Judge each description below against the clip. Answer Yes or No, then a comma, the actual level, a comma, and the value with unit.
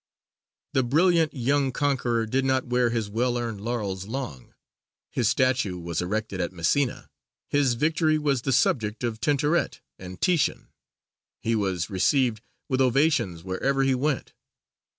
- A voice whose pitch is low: Yes, low, 125 Hz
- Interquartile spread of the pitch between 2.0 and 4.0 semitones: No, average, 4.7 semitones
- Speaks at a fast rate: No, average, 140 wpm